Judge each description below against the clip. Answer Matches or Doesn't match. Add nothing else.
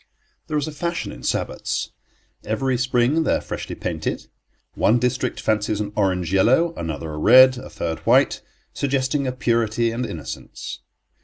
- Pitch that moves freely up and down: Doesn't match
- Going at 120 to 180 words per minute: Matches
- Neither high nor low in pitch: Doesn't match